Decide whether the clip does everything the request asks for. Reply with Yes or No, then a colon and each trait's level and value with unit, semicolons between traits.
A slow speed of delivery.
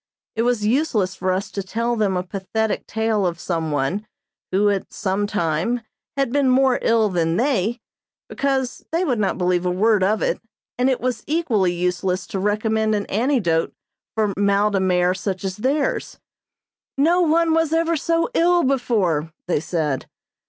No: average, 170 wpm